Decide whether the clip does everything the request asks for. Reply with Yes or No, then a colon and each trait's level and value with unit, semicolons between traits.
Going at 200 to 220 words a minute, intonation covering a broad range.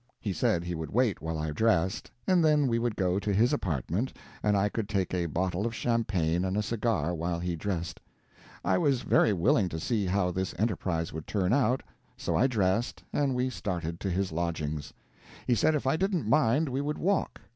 Yes: fast, 205 wpm; wide, 5.9 semitones